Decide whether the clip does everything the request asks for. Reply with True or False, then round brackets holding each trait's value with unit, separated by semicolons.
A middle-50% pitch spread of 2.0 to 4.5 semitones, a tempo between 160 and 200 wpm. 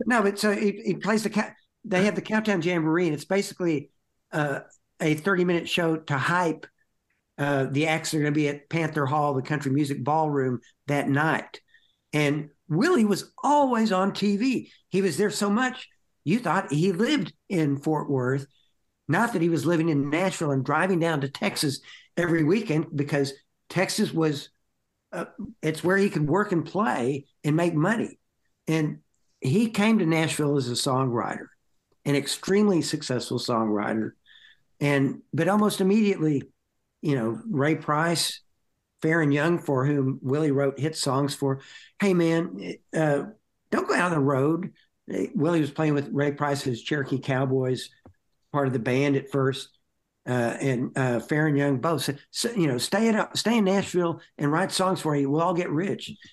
False (4.9 semitones; 175 wpm)